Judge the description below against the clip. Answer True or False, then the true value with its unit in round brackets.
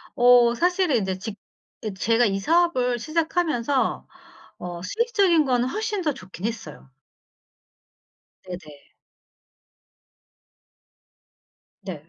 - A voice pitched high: True (245 Hz)